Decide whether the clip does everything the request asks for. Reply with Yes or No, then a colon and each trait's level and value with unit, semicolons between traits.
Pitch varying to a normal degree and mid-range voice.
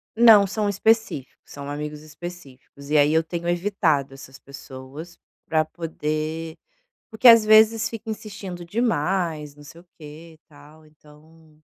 Yes: average, 4.8 semitones; medium, 160 Hz